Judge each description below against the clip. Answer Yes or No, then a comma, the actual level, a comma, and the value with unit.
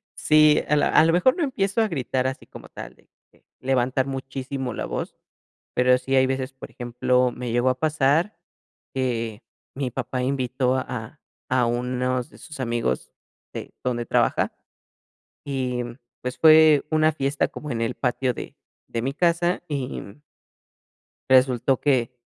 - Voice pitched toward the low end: Yes, low, 130 Hz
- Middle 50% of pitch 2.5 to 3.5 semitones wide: Yes, average, 2.8 semitones